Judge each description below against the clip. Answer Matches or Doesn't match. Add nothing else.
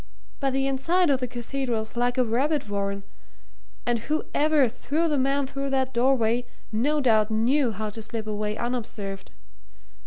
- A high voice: Matches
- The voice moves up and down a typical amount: Matches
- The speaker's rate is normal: Matches